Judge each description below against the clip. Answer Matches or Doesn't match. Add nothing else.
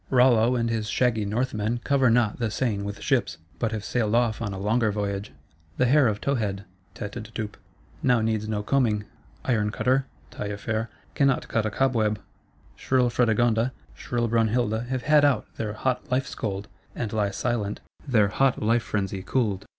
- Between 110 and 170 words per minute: Matches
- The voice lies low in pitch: Matches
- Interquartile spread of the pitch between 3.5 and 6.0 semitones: Doesn't match